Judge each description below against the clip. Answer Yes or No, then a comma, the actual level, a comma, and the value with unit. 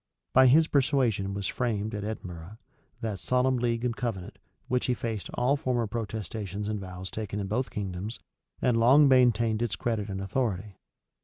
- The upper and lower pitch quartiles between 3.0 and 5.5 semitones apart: Yes, average, 3.7 semitones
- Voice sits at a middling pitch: No, low, 110 Hz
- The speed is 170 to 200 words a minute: No, average, 160 wpm